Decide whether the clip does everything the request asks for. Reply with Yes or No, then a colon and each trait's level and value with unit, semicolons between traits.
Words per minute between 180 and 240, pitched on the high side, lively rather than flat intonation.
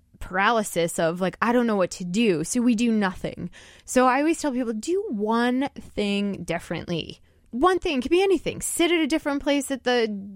Yes: fast, 205 wpm; high, 230 Hz; wide, 7.0 semitones